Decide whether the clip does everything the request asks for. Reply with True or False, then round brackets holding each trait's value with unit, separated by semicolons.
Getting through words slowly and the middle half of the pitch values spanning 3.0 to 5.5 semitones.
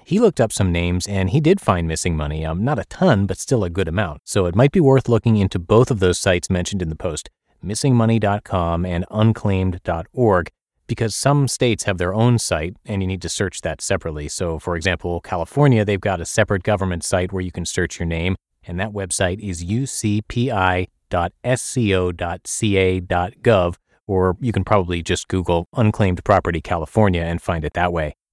False (185 wpm; 3.7 semitones)